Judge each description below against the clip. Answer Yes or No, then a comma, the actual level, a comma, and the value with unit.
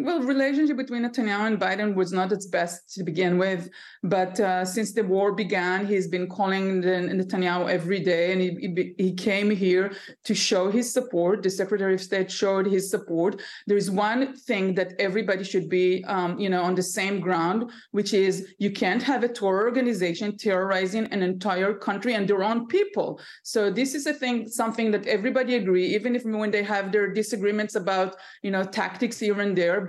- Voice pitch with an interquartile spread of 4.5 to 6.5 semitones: No, average, 3.0 semitones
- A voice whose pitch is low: No, high, 200 Hz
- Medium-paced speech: Yes, average, 195 wpm